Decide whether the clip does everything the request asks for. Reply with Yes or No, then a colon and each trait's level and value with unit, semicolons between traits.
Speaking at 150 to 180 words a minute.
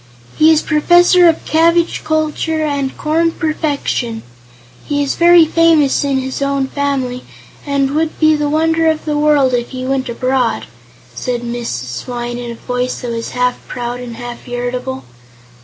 Yes: average, 160 wpm